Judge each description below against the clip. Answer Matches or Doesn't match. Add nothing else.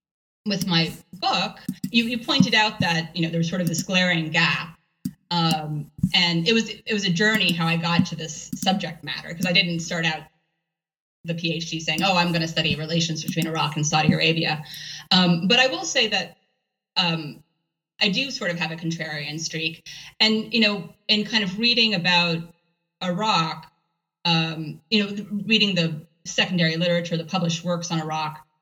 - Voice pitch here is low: Doesn't match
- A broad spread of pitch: Doesn't match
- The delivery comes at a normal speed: Matches